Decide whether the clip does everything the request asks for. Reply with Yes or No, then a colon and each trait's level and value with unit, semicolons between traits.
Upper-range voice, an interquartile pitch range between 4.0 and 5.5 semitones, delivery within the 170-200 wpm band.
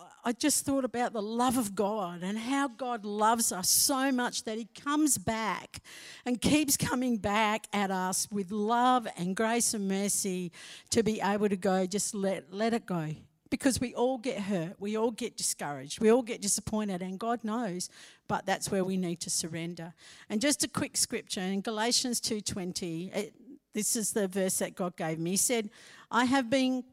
Yes: high, 215 Hz; average, 4.3 semitones; average, 190 wpm